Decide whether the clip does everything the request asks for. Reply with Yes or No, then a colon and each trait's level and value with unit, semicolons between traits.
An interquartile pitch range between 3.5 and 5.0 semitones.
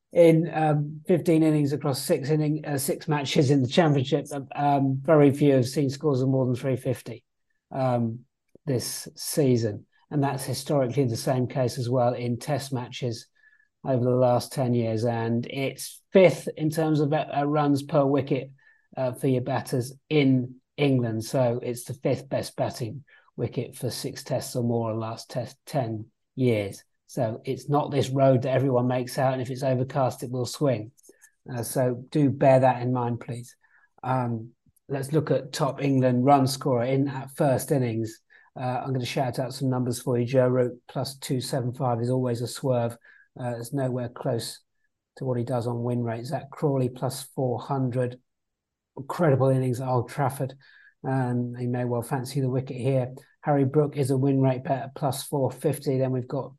No: narrow, 2.4 semitones